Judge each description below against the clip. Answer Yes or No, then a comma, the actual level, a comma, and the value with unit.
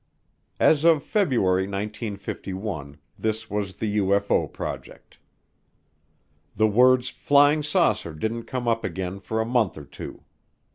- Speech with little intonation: No, average, 4.5 semitones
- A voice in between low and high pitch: No, low, 110 Hz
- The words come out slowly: Yes, slow, 125 wpm